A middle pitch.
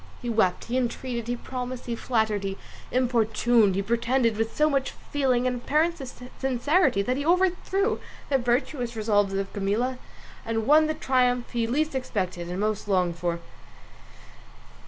No: high, 240 Hz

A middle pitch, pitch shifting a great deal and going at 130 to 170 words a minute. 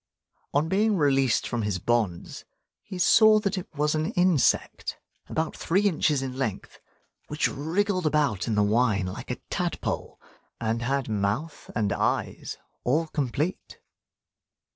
Yes: medium, 145 Hz; wide, 6.6 semitones; average, 140 wpm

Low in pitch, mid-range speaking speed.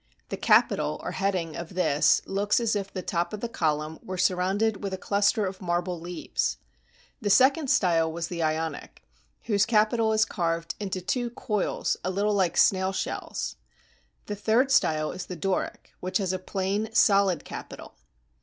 No: high, 190 Hz; average, 170 wpm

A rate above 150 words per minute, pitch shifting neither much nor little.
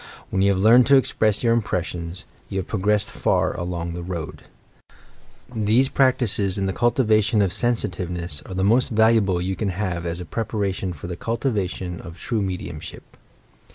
Yes: average, 170 wpm; average, 3.9 semitones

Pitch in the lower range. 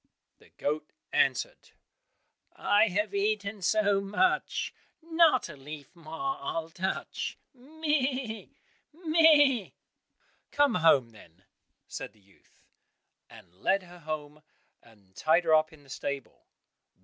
No: high, 190 Hz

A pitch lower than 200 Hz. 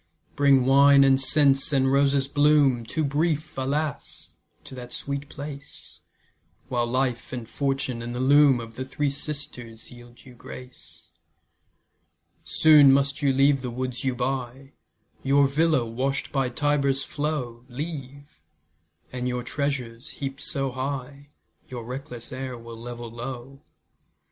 Yes: low, 135 Hz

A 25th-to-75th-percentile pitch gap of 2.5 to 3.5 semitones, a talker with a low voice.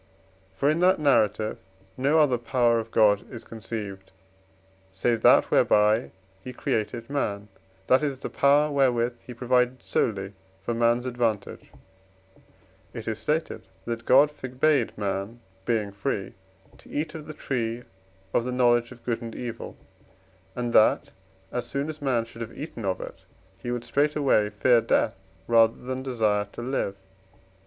Yes: average, 2.9 semitones; low, 120 Hz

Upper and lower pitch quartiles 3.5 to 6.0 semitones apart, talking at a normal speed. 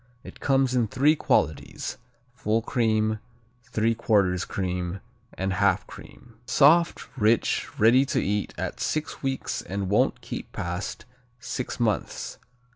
No: average, 4.5 semitones; slow, 120 wpm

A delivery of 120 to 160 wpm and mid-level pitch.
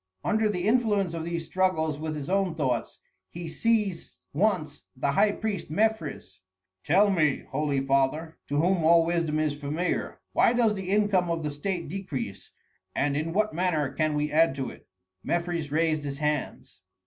No: average, 170 wpm; medium, 165 Hz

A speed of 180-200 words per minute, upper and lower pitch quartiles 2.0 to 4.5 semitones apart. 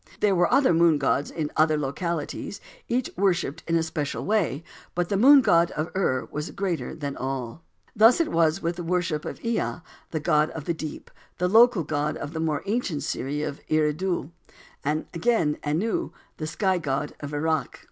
Yes: average, 190 wpm; average, 3.7 semitones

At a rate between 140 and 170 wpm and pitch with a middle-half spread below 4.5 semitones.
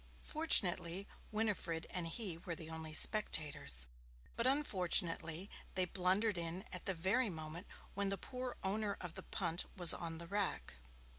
Yes: average, 150 wpm; average, 3.6 semitones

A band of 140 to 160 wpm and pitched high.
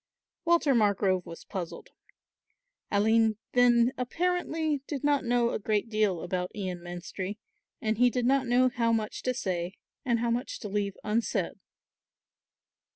Yes: average, 145 wpm; high, 230 Hz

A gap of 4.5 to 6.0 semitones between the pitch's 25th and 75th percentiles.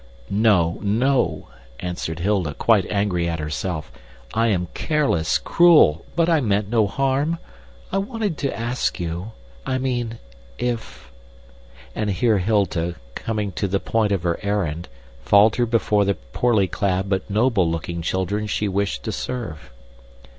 Yes: average, 5.1 semitones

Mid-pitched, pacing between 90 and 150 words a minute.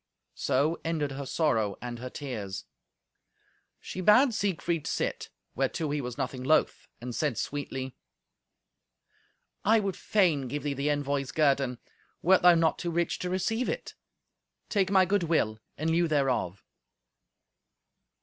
Yes: medium, 150 Hz; average, 140 wpm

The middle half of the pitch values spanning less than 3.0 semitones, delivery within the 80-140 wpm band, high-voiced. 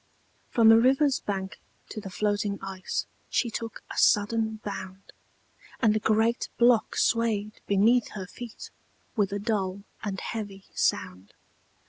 Yes: narrow, 2.6 semitones; slow, 135 wpm; high, 210 Hz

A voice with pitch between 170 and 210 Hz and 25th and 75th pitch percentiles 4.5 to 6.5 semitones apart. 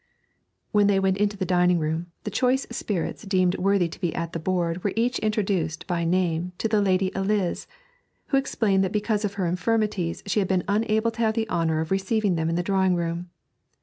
No: high, 190 Hz; average, 3.2 semitones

